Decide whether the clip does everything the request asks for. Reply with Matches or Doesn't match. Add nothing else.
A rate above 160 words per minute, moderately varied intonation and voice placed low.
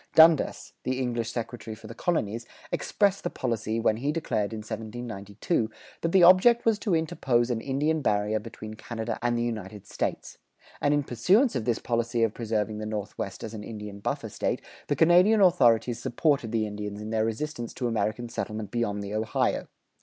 Matches